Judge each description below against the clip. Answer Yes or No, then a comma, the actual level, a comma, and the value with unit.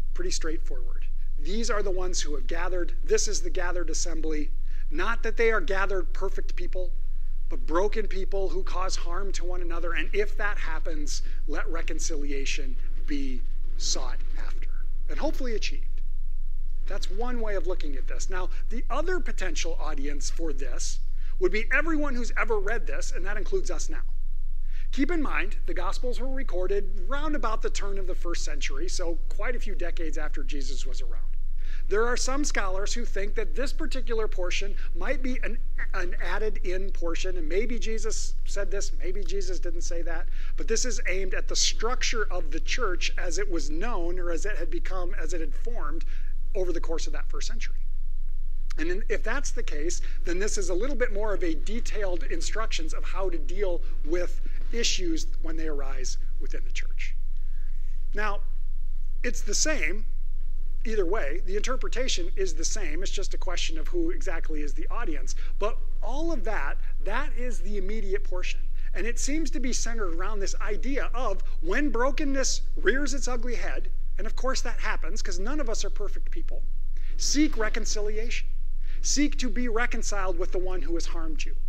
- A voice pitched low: No, high, 210 Hz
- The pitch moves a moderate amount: No, wide, 8.4 semitones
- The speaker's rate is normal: Yes, average, 180 wpm